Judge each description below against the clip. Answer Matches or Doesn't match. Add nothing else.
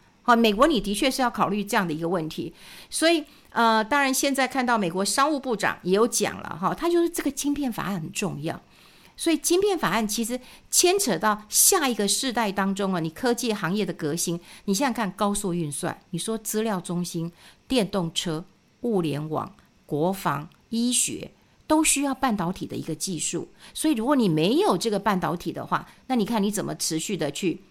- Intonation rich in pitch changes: Matches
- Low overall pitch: Doesn't match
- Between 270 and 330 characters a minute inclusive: Matches